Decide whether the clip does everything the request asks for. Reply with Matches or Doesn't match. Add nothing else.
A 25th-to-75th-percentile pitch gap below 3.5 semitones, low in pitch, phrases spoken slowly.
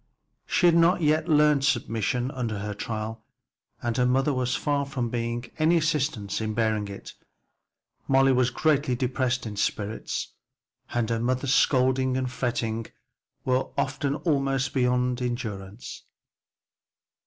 Matches